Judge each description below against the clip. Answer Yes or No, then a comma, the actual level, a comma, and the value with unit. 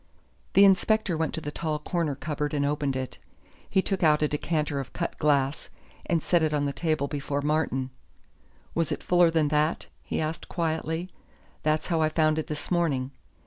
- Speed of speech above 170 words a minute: Yes, average, 185 wpm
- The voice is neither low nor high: Yes, medium, 155 Hz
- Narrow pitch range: Yes, narrow, 2.2 semitones